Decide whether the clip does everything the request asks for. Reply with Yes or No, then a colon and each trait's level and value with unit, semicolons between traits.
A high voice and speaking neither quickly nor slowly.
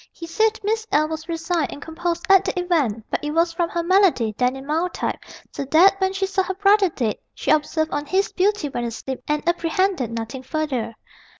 No: very high, 330 Hz; fast, 210 wpm